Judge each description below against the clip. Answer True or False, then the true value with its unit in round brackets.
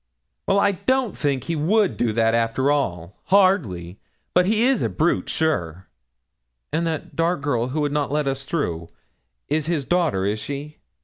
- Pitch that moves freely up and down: True (7.0 semitones)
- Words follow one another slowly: False (175 wpm)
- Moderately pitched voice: True (145 Hz)